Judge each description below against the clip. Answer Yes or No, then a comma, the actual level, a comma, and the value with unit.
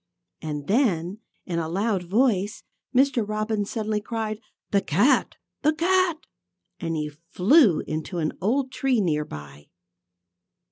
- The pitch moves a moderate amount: No, wide, 6.9 semitones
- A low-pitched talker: No, high, 205 Hz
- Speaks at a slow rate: Yes, slow, 130 wpm